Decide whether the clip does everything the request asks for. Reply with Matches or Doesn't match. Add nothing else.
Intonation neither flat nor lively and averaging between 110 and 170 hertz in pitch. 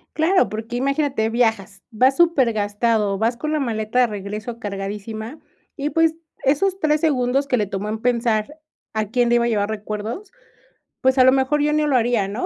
Doesn't match